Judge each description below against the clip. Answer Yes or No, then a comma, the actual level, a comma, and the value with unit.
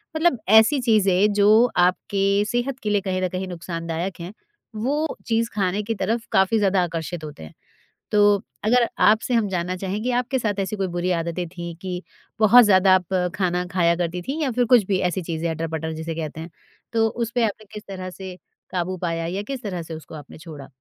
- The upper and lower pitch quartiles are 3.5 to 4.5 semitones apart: Yes, average, 3.9 semitones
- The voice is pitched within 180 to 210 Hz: Yes, high, 190 Hz